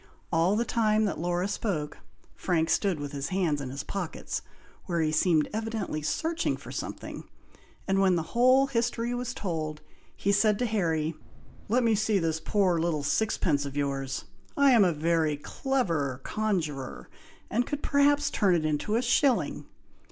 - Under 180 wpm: Yes, average, 165 wpm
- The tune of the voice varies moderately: No, wide, 6.4 semitones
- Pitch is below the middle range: No, medium, 185 Hz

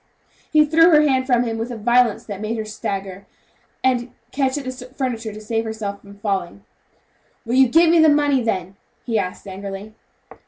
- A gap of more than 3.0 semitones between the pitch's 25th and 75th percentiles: Yes, average, 4.3 semitones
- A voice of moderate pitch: No, high, 230 Hz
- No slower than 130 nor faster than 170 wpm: No, average, 190 wpm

